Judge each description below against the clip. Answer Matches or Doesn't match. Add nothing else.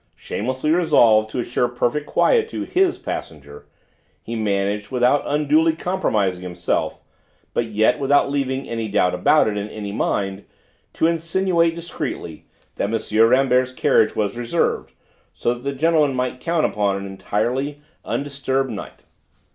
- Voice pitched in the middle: Doesn't match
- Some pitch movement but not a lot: Doesn't match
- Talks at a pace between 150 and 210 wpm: Doesn't match